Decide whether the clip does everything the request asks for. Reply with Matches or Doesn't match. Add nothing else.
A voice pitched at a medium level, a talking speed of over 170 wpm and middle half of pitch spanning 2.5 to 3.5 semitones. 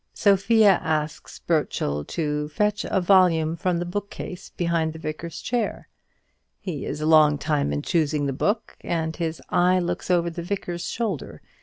Doesn't match